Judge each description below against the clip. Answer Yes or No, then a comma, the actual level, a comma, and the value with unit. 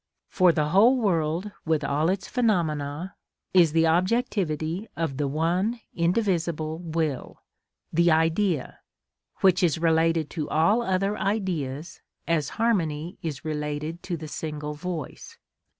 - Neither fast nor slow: No, slow, 125 wpm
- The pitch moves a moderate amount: Yes, average, 3.3 semitones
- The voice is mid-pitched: Yes, medium, 165 Hz